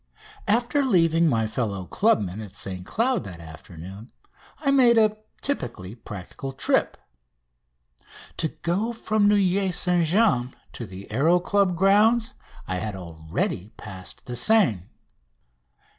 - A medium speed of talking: No, slow, 125 wpm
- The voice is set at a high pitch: No, medium, 160 Hz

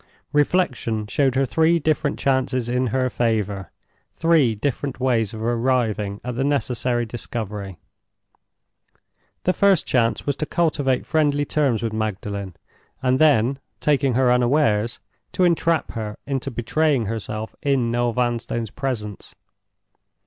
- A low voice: Yes, low, 125 Hz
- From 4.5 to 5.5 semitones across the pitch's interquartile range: No, average, 4.1 semitones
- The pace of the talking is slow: Yes, slow, 125 wpm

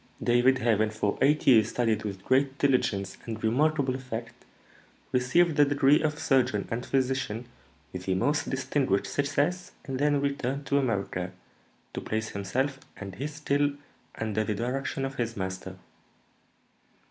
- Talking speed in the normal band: Yes, average, 145 wpm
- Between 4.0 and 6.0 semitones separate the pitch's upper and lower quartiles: Yes, average, 4.5 semitones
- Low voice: Yes, low, 130 Hz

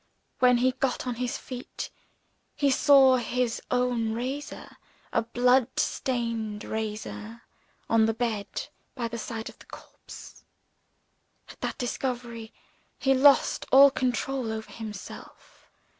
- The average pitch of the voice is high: Yes, high, 245 Hz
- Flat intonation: Yes, narrow, 2.3 semitones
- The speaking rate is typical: No, slow, 125 wpm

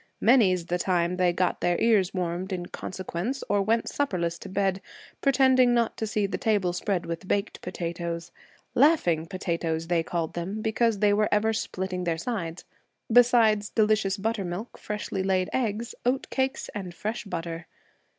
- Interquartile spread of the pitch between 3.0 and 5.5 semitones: Yes, average, 4.1 semitones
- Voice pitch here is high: Yes, high, 195 Hz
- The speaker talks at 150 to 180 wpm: Yes, average, 160 wpm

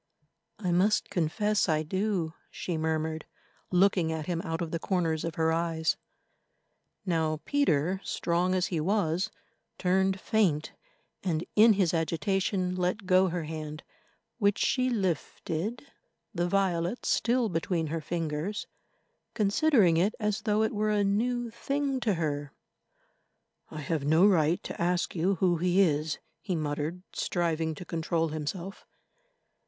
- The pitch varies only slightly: No, average, 3.8 semitones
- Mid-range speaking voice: Yes, medium, 175 Hz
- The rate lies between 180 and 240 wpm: No, average, 140 wpm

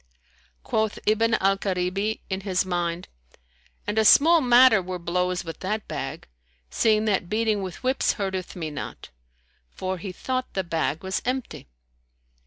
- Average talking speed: Yes, average, 150 wpm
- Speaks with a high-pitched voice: Yes, high, 195 Hz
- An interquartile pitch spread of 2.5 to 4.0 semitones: Yes, average, 3.3 semitones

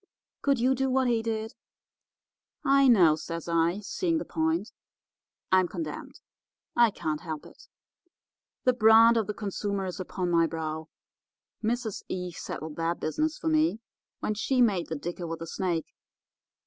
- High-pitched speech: Yes, high, 200 Hz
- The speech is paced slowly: No, average, 155 wpm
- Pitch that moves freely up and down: Yes, wide, 6.6 semitones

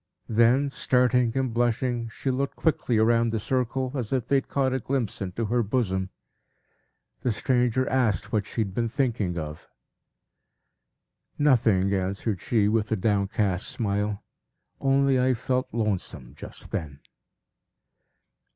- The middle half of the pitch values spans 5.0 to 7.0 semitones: No, average, 4.2 semitones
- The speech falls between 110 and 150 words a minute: Yes, slow, 135 wpm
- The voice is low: Yes, low, 115 Hz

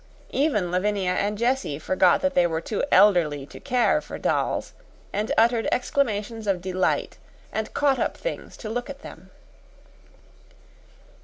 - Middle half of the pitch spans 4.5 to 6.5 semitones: Yes, average, 5.1 semitones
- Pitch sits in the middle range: No, high, 210 Hz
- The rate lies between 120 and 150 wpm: Yes, average, 145 wpm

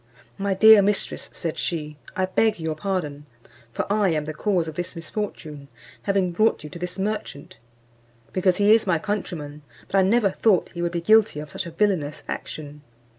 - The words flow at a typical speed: Yes, average, 185 wpm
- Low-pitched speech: No, medium, 180 Hz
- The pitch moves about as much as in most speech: Yes, average, 4.7 semitones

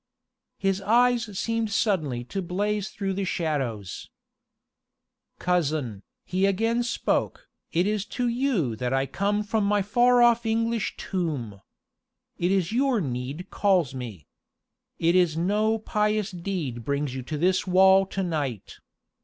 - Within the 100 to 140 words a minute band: Yes, slow, 135 wpm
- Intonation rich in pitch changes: Yes, wide, 6.1 semitones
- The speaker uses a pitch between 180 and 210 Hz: Yes, high, 190 Hz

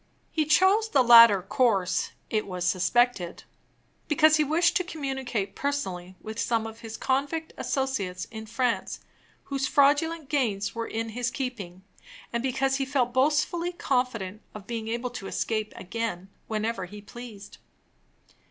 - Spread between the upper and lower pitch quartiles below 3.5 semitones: No, average, 4.6 semitones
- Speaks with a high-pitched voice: Yes, high, 240 Hz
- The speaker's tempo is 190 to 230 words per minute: No, average, 145 wpm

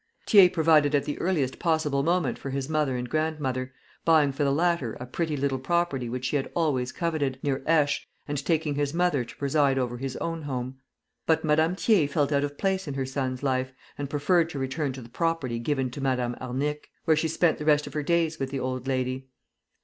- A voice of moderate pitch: Yes, medium, 145 Hz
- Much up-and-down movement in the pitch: No, average, 3.2 semitones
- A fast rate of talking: Yes, fast, 215 wpm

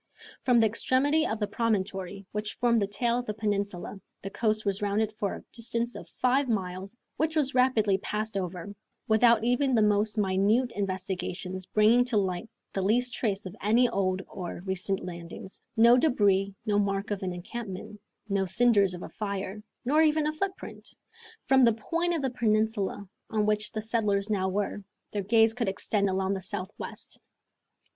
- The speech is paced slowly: No, average, 175 wpm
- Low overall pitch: No, high, 210 Hz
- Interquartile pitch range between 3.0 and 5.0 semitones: Yes, average, 3.3 semitones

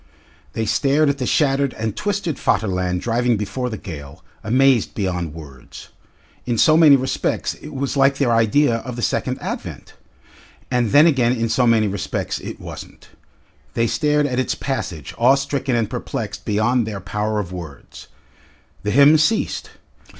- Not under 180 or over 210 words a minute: No, average, 160 wpm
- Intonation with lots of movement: No, average, 4.8 semitones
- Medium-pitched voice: No, low, 120 Hz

